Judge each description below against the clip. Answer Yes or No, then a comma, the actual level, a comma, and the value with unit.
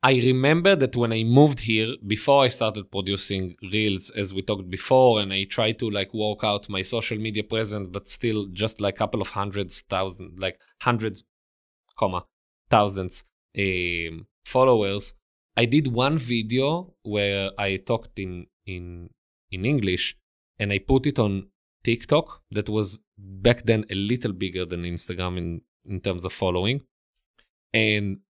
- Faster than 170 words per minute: No, average, 155 wpm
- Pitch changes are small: No, average, 3.3 semitones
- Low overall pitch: Yes, low, 105 Hz